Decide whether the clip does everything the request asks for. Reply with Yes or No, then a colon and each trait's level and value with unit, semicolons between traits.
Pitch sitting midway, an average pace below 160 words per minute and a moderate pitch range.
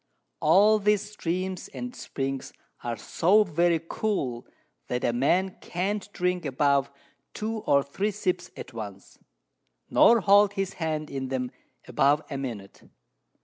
No: medium, 170 Hz; slow, 135 wpm; wide, 6.8 semitones